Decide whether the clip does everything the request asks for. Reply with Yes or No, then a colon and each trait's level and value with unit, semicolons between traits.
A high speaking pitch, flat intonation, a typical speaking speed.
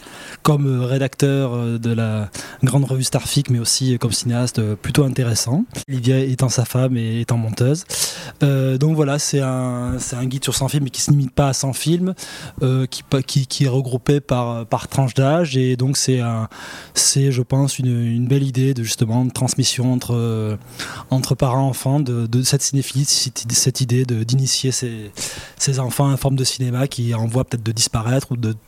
No: low, 130 Hz; narrow, 2.1 semitones; average, 185 wpm